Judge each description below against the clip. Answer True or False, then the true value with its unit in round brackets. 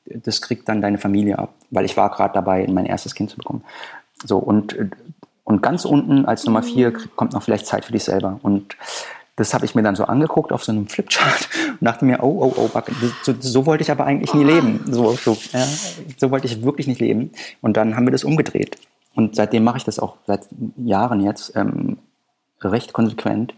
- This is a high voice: False (115 Hz)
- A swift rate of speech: True (215 wpm)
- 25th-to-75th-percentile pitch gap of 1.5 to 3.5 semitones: False (4.1 semitones)